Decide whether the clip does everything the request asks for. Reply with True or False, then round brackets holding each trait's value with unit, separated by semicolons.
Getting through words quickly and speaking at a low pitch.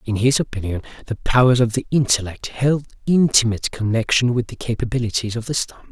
False (170 wpm; 120 Hz)